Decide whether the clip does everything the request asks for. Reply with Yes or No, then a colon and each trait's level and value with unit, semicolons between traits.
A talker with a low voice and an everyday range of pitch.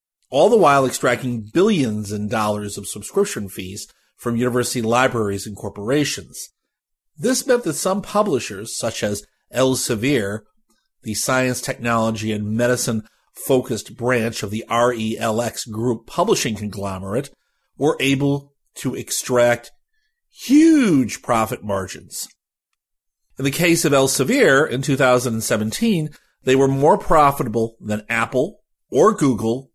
Yes: low, 120 Hz; average, 4.1 semitones